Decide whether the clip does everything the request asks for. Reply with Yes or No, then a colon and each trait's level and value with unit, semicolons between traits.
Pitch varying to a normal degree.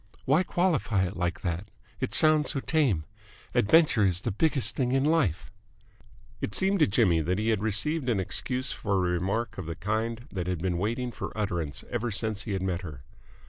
No: wide, 6.0 semitones